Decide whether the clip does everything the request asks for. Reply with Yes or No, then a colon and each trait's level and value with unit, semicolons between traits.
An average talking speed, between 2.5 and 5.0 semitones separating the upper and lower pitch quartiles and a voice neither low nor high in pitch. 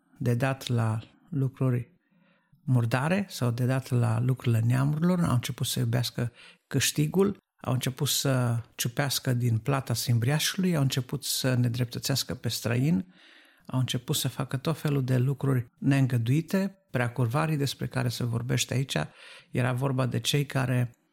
No: average, 140 wpm; average, 2.9 semitones; low, 130 Hz